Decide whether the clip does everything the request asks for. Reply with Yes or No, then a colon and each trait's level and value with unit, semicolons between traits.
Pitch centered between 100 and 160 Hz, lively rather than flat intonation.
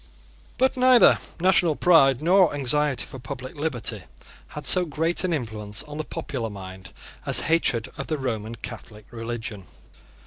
Yes: low, 135 Hz; wide, 6.1 semitones